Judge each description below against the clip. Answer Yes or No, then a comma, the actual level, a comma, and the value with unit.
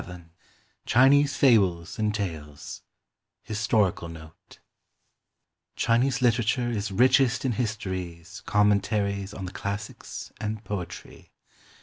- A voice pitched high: No, low, 105 Hz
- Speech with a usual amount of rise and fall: Yes, average, 4.2 semitones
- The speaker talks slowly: Yes, slow, 95 wpm